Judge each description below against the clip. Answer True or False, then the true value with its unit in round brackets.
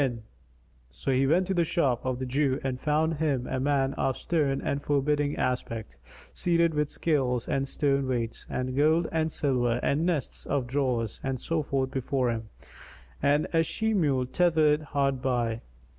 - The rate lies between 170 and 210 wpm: True (175 wpm)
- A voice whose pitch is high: False (140 Hz)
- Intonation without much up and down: False (3.1 semitones)